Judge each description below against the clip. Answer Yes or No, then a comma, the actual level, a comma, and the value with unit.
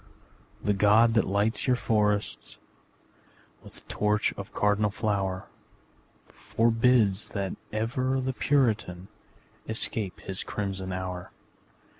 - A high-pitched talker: No, low, 105 Hz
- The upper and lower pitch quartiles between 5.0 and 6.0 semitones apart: No, average, 2.7 semitones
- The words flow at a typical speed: No, slow, 100 wpm